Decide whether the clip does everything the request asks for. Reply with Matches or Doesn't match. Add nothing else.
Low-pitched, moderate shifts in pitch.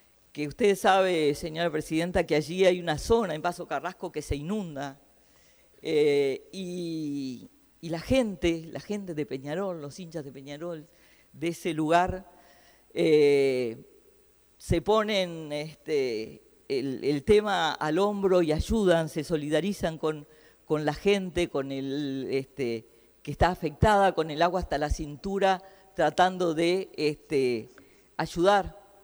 Doesn't match